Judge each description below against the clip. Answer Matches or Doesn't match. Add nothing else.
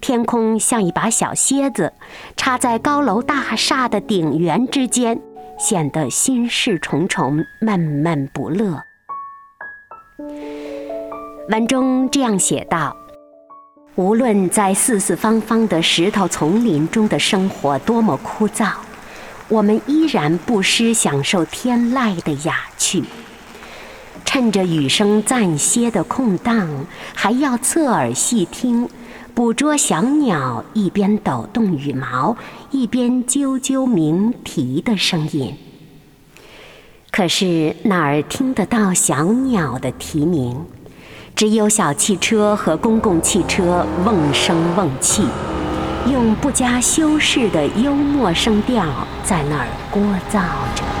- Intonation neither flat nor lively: Doesn't match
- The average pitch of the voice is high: Matches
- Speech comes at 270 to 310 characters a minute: Doesn't match